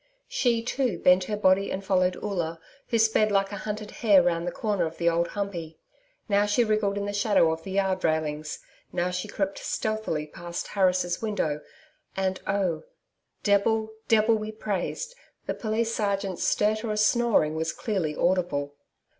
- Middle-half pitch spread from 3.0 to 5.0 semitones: Yes, average, 3.6 semitones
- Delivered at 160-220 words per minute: Yes, average, 165 wpm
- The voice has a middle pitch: No, high, 195 Hz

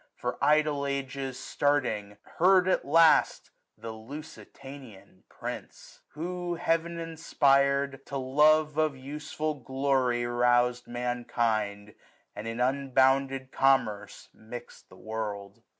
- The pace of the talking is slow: Yes, slow, 110 wpm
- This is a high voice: No, low, 135 Hz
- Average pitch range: Yes, average, 3.7 semitones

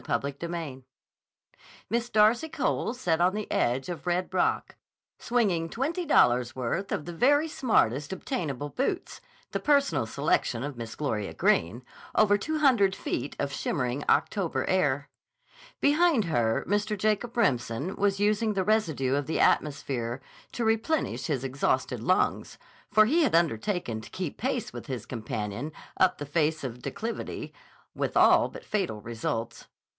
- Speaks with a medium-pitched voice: Yes, medium, 170 Hz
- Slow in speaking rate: No, average, 150 wpm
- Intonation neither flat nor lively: No, wide, 8.7 semitones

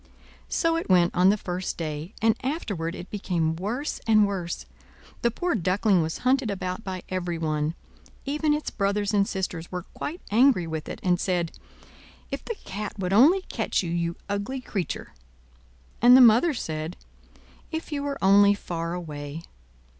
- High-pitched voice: Yes, high, 195 Hz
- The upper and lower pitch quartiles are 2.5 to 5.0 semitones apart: No, wide, 5.5 semitones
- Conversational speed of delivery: Yes, average, 160 wpm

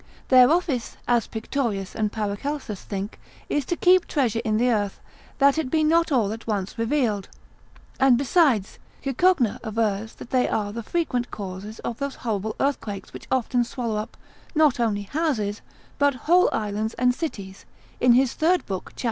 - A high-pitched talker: Yes, high, 235 Hz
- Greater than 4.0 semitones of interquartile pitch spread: Yes, average, 4.9 semitones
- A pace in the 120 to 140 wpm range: No, average, 165 wpm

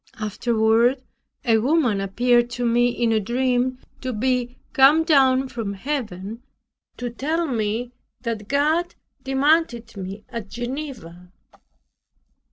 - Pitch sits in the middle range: No, high, 245 Hz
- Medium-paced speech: No, slow, 115 wpm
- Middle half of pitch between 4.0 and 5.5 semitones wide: No, average, 3.3 semitones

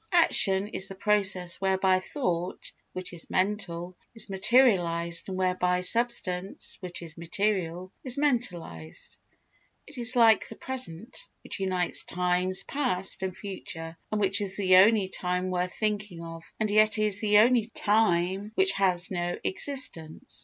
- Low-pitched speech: No, high, 190 Hz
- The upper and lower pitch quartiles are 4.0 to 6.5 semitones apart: No, average, 3.1 semitones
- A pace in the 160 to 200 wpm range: No, average, 145 wpm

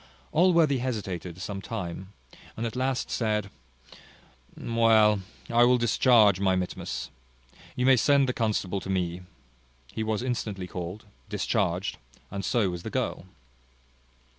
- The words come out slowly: Yes, slow, 130 wpm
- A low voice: Yes, low, 110 Hz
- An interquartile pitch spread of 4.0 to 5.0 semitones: Yes, average, 4.3 semitones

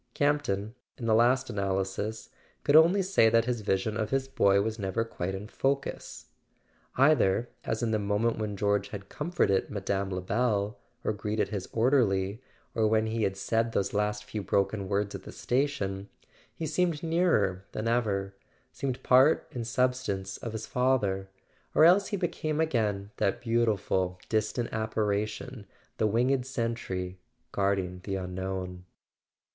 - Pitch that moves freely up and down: No, average, 4.2 semitones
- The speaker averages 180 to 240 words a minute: No, average, 150 wpm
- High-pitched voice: No, low, 110 Hz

